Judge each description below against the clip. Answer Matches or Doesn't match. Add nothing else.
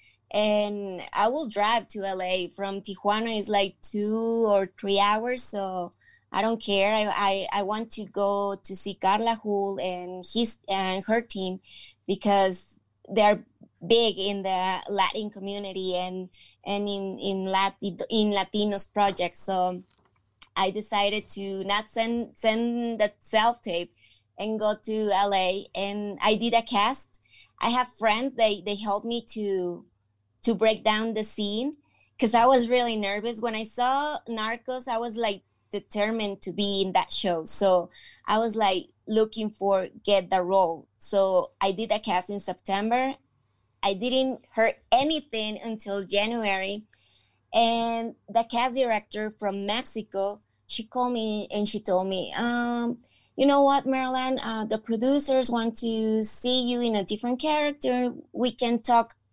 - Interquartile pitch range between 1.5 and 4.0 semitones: Matches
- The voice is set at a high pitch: Matches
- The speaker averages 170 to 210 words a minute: Doesn't match